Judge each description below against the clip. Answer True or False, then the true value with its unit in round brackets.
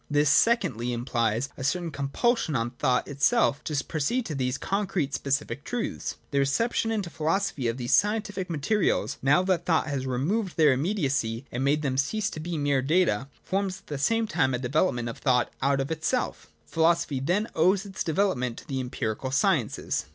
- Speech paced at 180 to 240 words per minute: True (185 wpm)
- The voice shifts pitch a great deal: True (6.0 semitones)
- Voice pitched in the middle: True (145 Hz)